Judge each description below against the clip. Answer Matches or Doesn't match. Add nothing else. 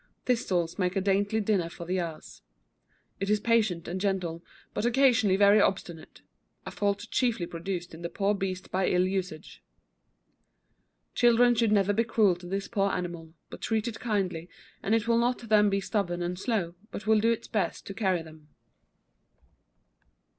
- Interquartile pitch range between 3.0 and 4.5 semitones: Matches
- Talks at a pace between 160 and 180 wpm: Matches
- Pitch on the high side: Matches